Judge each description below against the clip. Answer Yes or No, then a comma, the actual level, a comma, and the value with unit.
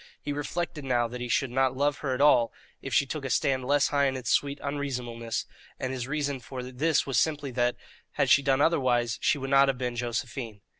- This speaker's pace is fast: Yes, fast, 220 wpm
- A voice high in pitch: No, low, 135 Hz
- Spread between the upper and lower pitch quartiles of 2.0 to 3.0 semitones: Yes, narrow, 2.6 semitones